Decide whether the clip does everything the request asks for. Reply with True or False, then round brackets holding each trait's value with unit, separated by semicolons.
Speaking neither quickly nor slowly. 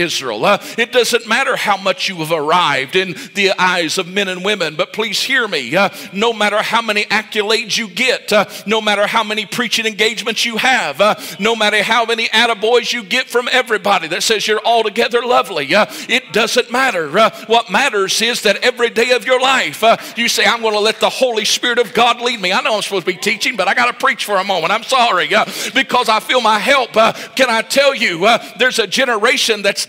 False (230 wpm)